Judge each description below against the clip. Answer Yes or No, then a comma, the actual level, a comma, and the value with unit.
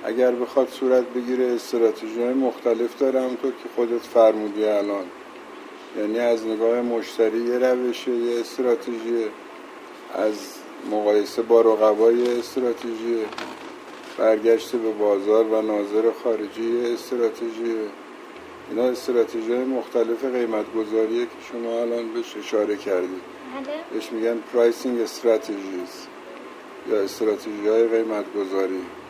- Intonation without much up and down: Yes, narrow, 2.1 semitones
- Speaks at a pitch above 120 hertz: No, low, 115 Hz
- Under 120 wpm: Yes, slow, 105 wpm